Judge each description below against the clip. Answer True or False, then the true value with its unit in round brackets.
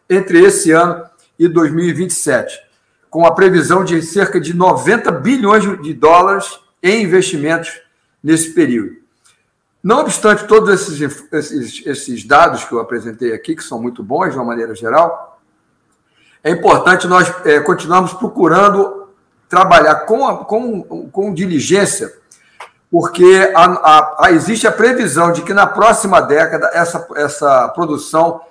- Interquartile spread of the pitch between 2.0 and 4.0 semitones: True (3.6 semitones)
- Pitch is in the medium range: True (180 Hz)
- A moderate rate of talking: True (135 wpm)